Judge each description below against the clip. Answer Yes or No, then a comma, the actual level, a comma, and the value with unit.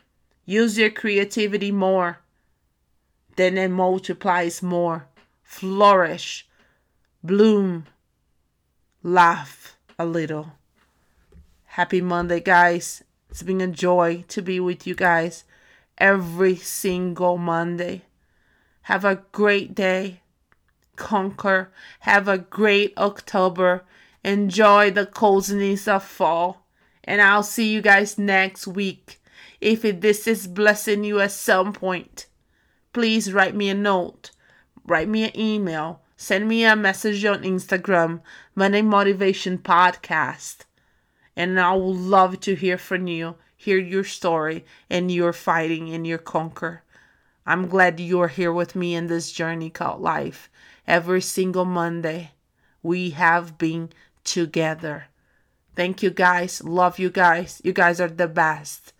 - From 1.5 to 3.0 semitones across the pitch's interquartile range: Yes, average, 2.7 semitones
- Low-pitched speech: No, medium, 185 Hz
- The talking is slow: Yes, slow, 125 wpm